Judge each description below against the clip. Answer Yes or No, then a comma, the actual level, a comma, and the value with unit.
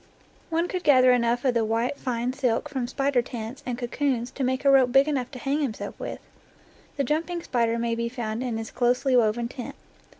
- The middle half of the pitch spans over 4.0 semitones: No, average, 2.8 semitones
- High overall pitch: Yes, very high, 250 Hz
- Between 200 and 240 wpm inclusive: Yes, fast, 205 wpm